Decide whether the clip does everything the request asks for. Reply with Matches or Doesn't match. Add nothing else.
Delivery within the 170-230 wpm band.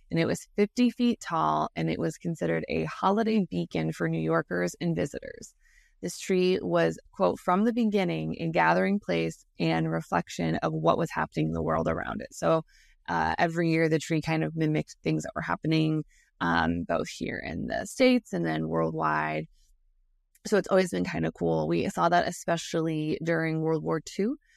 Matches